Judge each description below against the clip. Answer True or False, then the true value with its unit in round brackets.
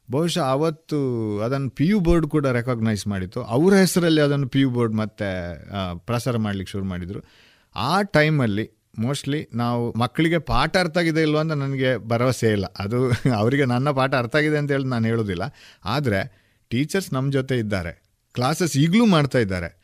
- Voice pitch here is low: True (125 Hz)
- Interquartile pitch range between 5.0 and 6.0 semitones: True (5.4 semitones)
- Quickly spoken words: True (155 wpm)